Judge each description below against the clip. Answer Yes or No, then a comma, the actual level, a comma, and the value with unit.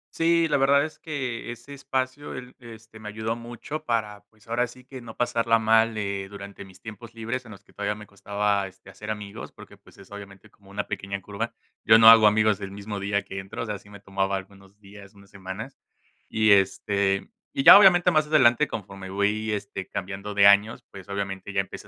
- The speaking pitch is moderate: No, low, 105 Hz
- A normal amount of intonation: Yes, average, 3.0 semitones